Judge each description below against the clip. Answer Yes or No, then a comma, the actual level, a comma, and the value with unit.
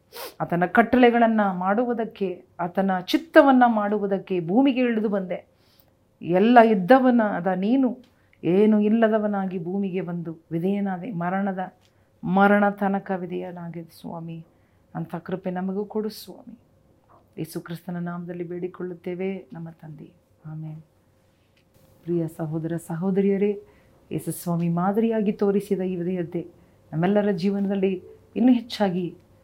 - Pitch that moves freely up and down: No, average, 3.4 semitones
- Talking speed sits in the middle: Yes, average, 95 wpm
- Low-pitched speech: No, medium, 185 Hz